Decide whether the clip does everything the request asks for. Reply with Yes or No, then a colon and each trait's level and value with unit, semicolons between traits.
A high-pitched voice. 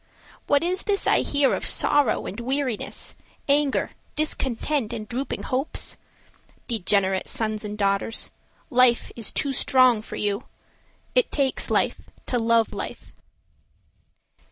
Yes: high, 245 Hz